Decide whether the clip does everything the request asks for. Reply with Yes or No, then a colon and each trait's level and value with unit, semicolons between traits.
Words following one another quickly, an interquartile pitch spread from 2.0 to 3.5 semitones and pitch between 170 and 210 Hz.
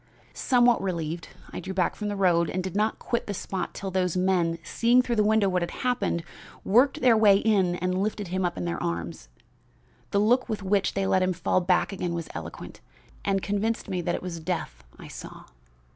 Yes: fast, 210 wpm; average, 3.2 semitones; high, 190 Hz